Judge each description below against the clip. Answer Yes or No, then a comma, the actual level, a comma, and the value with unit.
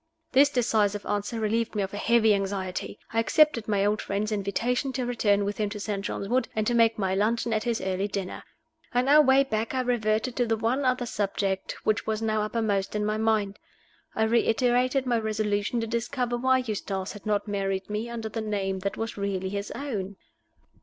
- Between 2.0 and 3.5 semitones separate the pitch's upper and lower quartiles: Yes, average, 2.8 semitones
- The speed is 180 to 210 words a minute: Yes, average, 200 wpm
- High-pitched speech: Yes, high, 215 Hz